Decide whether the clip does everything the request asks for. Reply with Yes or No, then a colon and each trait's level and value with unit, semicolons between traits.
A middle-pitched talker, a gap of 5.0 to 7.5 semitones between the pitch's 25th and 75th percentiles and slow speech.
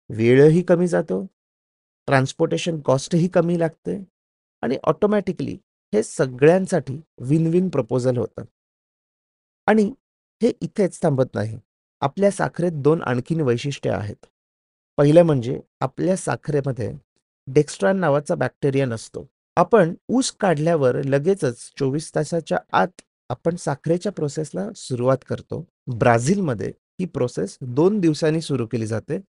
No: medium, 150 Hz; wide, 5.5 semitones; average, 110 wpm